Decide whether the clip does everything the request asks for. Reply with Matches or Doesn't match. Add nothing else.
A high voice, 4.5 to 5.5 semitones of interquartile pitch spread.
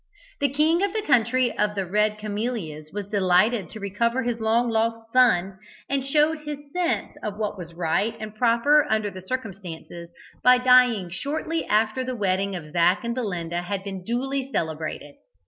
Matches